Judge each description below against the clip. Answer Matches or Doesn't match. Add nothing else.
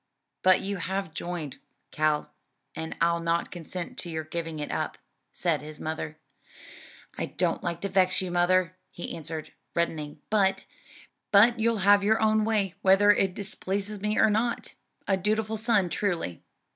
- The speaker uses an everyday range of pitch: Matches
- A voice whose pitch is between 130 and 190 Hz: Matches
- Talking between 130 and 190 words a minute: Matches